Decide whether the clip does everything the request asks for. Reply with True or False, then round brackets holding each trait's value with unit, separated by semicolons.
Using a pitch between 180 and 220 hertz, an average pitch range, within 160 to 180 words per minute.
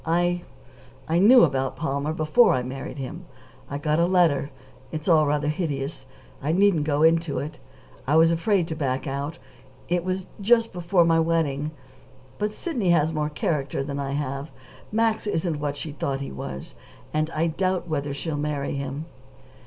False (155 Hz; 3.5 semitones; 170 wpm)